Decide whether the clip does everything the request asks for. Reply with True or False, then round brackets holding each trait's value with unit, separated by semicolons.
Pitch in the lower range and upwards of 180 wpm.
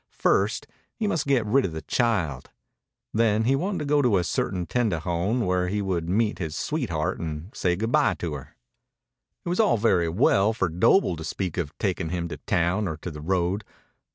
True (95 Hz; 200 wpm)